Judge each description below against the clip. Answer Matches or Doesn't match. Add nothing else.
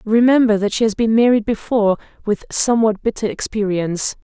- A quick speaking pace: Doesn't match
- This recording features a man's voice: Doesn't match